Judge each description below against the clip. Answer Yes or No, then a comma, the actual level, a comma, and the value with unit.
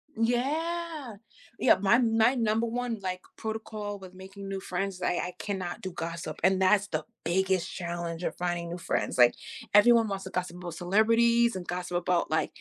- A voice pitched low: No, high, 190 Hz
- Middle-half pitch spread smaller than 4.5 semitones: Yes, average, 4.1 semitones